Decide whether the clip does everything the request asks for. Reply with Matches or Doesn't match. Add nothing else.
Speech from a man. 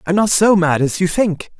Matches